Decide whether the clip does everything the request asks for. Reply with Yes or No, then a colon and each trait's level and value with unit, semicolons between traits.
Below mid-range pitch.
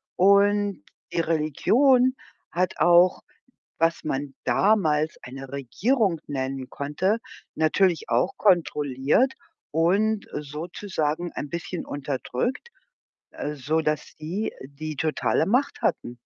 No: medium, 160 Hz